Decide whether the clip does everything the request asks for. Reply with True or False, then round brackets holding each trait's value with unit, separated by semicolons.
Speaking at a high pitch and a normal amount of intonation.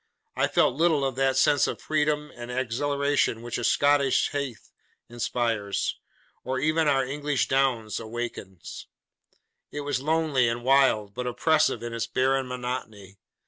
False (130 Hz; 3.4 semitones)